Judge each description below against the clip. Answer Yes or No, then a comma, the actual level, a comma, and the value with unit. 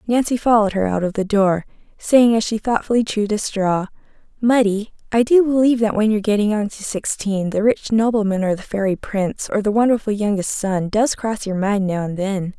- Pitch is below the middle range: No, high, 210 Hz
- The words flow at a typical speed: No, fast, 210 wpm